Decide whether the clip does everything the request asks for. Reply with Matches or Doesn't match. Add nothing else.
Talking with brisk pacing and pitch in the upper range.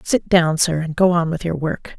Doesn't match